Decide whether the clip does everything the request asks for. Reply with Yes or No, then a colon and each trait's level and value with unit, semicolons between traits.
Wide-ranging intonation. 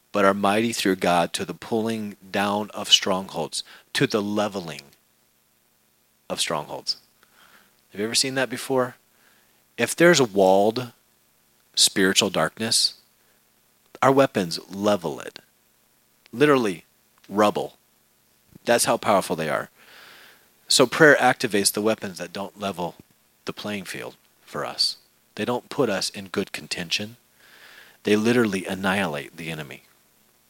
No: average, 3.4 semitones